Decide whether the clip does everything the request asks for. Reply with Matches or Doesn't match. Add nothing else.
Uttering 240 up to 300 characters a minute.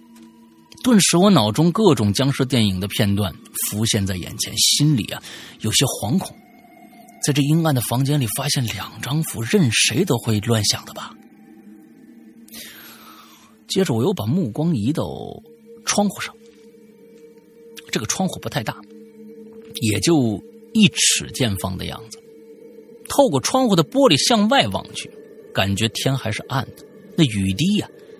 Doesn't match